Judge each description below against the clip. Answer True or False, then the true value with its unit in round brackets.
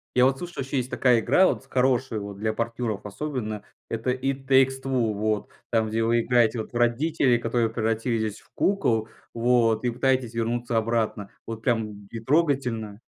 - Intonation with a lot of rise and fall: False (2.8 semitones)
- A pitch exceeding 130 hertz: False (120 Hz)